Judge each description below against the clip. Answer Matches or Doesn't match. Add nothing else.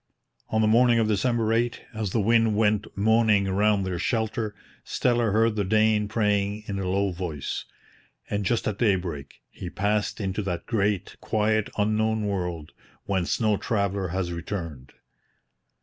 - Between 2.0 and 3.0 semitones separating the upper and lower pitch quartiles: Matches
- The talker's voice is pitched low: Matches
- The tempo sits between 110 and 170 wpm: Matches